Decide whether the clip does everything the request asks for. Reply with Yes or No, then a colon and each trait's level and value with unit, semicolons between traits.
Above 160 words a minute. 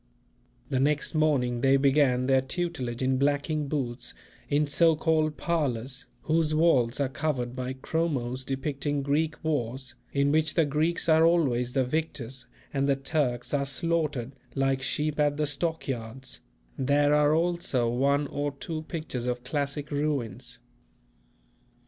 No: average, 140 wpm